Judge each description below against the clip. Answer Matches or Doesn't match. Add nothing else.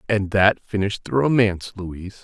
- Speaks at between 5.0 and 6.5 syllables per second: Matches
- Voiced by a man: Matches